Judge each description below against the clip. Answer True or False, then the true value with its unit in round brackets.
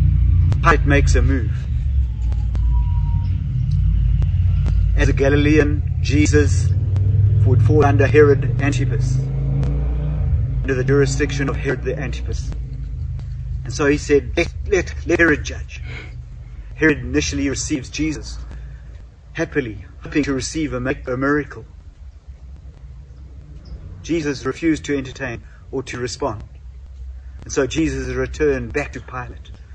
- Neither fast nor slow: False (105 wpm)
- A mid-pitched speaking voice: False (95 Hz)